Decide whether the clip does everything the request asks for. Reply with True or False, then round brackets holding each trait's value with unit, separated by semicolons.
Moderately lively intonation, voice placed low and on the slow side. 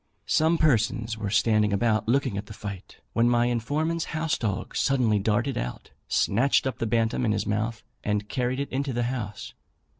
False (3.6 semitones; 115 Hz; 180 wpm)